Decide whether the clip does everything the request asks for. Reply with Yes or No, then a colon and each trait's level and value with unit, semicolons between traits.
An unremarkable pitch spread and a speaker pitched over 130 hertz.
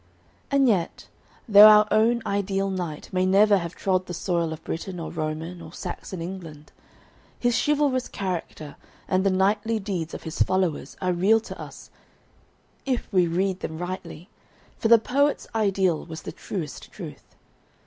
Yes: average, 3.8 semitones; medium, 185 Hz